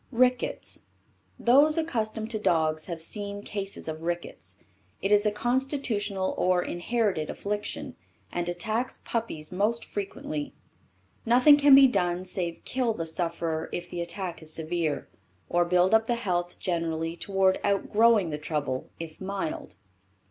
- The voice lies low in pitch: No, high, 190 Hz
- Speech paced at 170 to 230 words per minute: No, average, 140 wpm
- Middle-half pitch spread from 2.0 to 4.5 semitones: No, average, 4.9 semitones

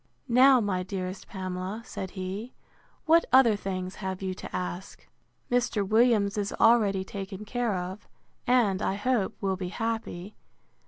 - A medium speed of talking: Yes, average, 145 wpm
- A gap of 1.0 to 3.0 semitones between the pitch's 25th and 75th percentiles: No, average, 3.5 semitones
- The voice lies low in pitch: No, high, 200 Hz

